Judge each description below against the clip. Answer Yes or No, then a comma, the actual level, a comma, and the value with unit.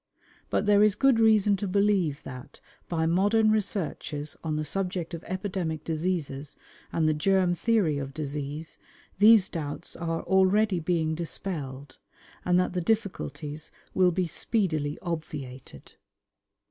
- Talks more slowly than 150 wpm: Yes, slow, 135 wpm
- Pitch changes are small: No, average, 4.4 semitones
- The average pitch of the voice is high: No, medium, 175 Hz